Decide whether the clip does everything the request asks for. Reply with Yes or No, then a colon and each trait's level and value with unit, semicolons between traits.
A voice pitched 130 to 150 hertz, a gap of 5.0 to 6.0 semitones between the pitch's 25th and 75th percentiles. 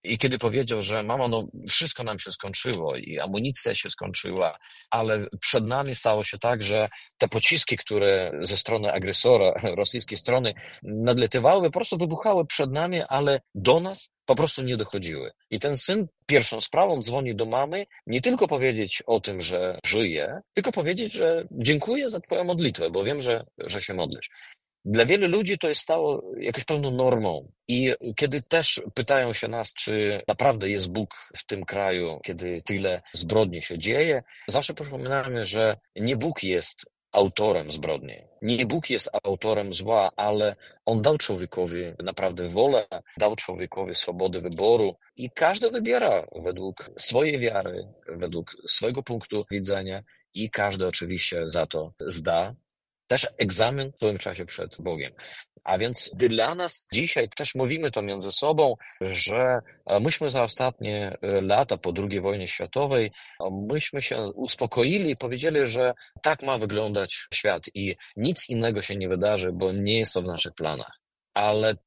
No: low, 115 Hz; wide, 5.6 semitones